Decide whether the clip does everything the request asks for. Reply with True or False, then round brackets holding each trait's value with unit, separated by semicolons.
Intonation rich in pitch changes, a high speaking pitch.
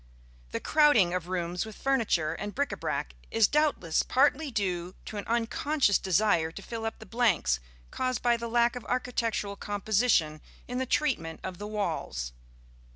True (5.8 semitones; 215 Hz)